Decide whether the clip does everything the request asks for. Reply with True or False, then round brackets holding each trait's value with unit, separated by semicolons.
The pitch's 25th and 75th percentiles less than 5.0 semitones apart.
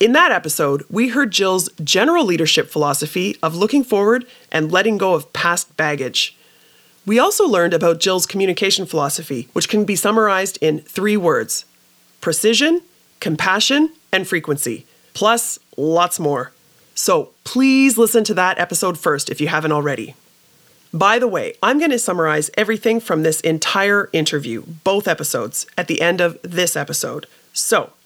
False (5.5 semitones)